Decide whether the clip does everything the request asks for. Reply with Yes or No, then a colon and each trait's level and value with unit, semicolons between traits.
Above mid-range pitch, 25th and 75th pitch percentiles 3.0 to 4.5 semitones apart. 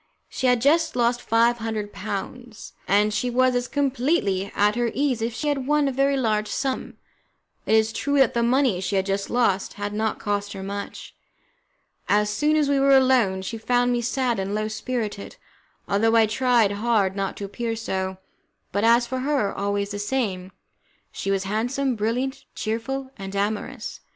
Yes: high, 230 Hz; average, 4.1 semitones